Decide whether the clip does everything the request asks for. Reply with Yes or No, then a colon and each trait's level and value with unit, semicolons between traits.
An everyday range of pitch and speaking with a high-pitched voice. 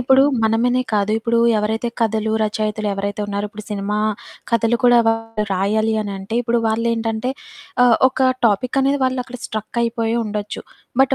No: narrow, 2.1 semitones; high, 225 Hz